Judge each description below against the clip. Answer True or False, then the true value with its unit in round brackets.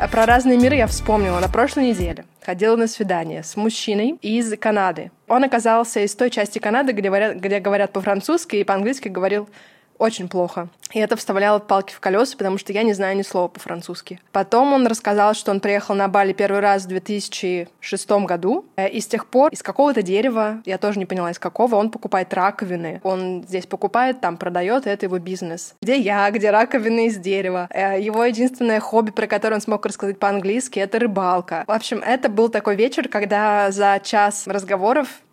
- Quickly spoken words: True (185 wpm)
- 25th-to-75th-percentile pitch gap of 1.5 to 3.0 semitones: True (2.7 semitones)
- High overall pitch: True (205 Hz)